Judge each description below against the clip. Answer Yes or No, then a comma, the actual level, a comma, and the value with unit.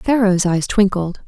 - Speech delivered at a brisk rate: No, average, 140 wpm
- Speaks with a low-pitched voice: No, high, 195 Hz